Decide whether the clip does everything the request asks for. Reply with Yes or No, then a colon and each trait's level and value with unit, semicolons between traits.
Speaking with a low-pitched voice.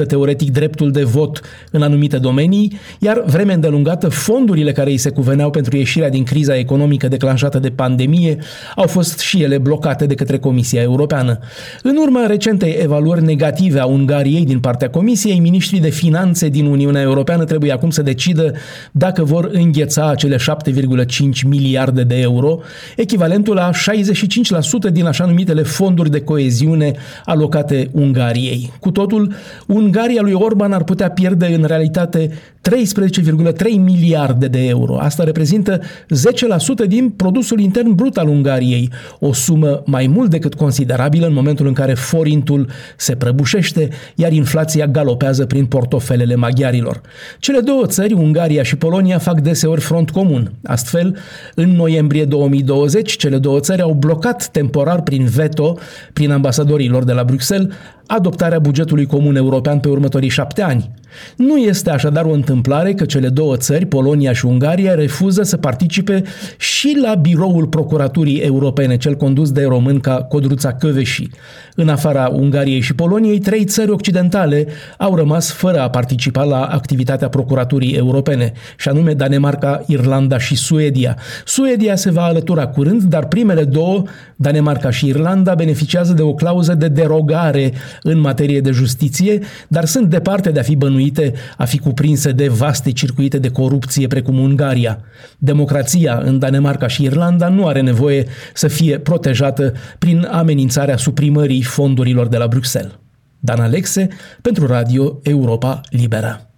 No: medium, 150 Hz